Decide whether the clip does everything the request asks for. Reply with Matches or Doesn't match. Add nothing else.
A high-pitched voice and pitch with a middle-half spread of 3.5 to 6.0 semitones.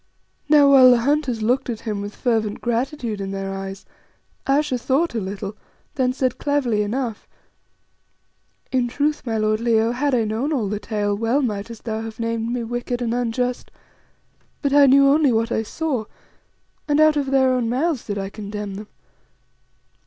Matches